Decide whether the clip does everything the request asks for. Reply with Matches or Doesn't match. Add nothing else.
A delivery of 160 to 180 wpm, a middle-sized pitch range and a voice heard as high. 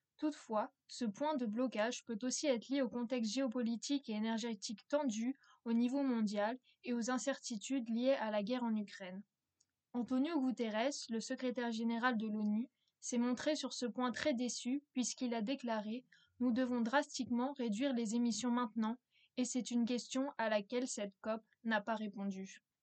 Doesn't match